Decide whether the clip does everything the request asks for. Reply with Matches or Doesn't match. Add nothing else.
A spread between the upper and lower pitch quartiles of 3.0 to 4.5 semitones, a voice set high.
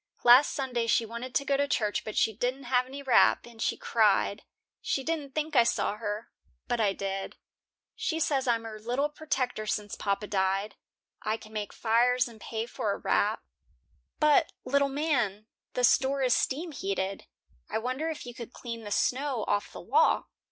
Matches